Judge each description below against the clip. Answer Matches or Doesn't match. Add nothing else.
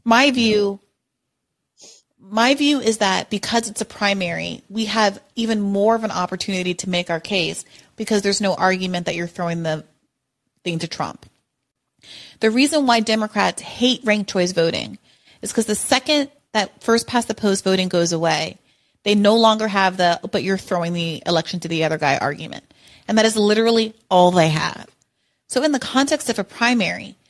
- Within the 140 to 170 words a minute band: Doesn't match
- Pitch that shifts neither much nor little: Matches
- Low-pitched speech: Doesn't match